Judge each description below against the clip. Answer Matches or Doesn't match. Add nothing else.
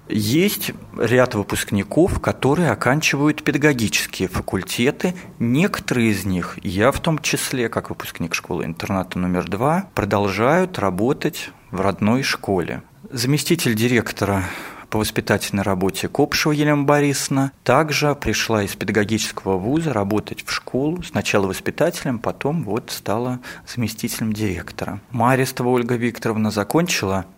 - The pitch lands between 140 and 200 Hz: Doesn't match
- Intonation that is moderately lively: Doesn't match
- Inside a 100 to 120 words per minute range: Matches